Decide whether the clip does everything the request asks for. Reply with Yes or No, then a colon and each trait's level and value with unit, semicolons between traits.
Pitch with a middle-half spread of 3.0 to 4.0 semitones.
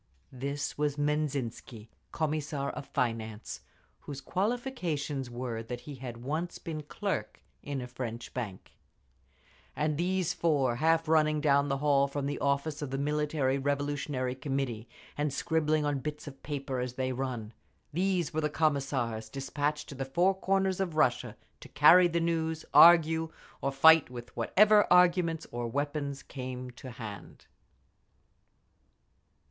Yes: average, 3.5 semitones